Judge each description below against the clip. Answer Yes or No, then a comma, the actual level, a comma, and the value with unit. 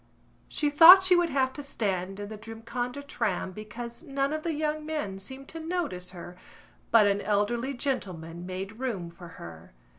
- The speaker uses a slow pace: No, average, 175 wpm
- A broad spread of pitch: Yes, wide, 7.1 semitones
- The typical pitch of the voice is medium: No, high, 235 Hz